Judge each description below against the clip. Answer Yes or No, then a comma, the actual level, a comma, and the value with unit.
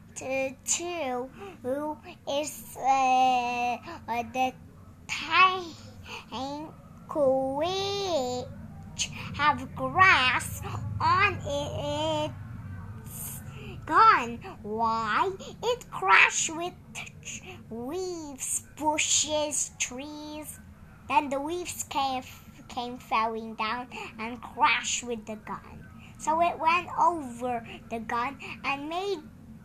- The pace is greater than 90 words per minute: No, slow, 85 wpm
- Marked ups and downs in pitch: No, average, 5.0 semitones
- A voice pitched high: Yes, very high, 265 Hz